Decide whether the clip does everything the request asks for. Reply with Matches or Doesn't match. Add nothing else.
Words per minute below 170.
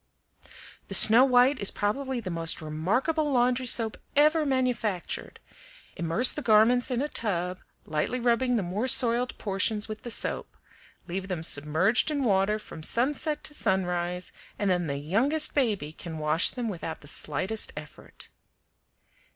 Matches